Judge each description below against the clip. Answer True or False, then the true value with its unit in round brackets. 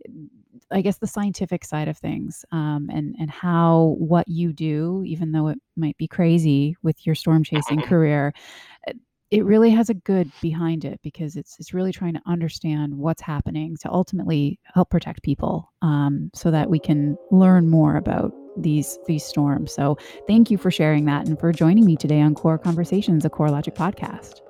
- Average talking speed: True (185 wpm)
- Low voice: False (165 Hz)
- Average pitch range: True (3.1 semitones)